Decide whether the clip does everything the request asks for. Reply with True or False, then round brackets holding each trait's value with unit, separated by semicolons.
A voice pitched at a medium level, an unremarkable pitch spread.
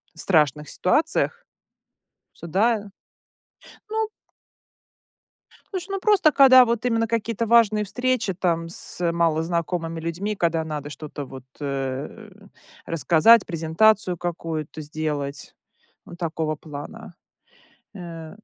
False (170 Hz; 6.1 semitones)